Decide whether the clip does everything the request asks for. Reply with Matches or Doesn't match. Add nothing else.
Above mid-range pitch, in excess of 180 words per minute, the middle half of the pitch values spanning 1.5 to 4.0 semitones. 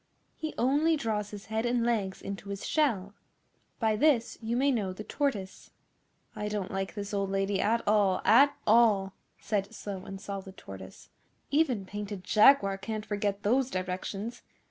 Doesn't match